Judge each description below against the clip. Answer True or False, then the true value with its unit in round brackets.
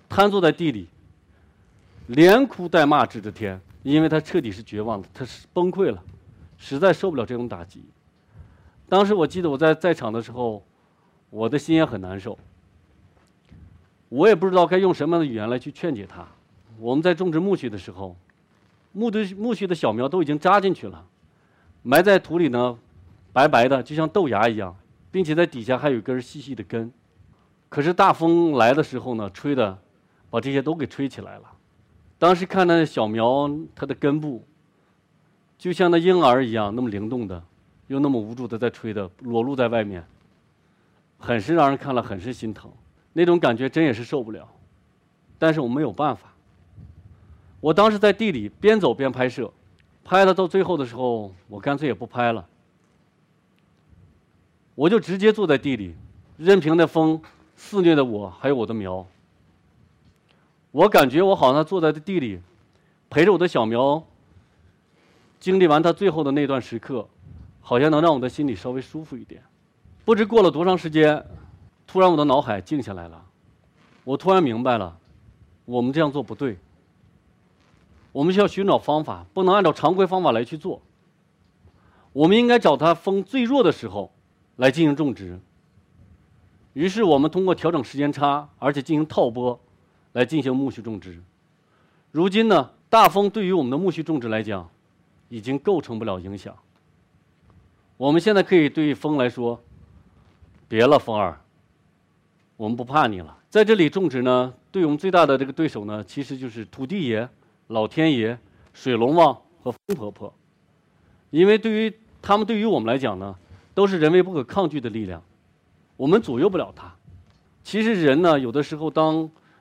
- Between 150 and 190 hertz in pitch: False (125 Hz)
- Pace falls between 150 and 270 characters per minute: True (255 characters per minute)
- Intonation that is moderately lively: False (8.3 semitones)